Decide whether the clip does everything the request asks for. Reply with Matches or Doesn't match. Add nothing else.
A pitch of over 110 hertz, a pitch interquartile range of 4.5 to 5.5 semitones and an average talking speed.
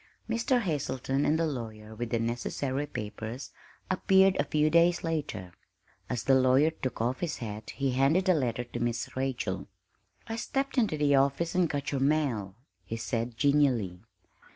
Matches